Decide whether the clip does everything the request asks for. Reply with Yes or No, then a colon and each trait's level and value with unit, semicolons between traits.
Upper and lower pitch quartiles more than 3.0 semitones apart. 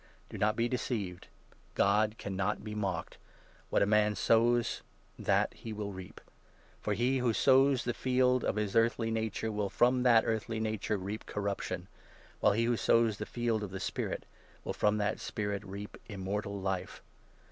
No: narrow, 2.5 semitones